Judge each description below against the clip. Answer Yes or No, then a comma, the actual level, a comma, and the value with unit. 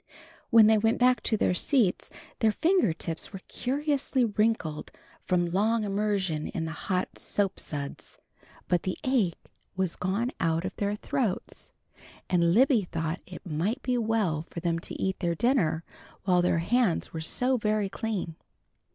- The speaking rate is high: No, average, 160 wpm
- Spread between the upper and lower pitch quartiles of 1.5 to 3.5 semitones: No, average, 5.0 semitones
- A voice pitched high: Yes, high, 195 Hz